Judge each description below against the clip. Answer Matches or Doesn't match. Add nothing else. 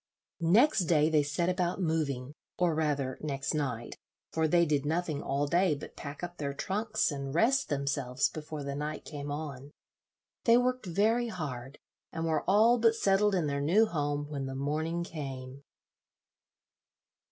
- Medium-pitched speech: Matches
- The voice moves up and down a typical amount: Matches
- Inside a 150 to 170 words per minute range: Matches